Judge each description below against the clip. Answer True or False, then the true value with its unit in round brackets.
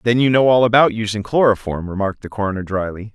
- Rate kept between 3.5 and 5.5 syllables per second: False (6.6 syllables/s)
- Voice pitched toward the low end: True (110 Hz)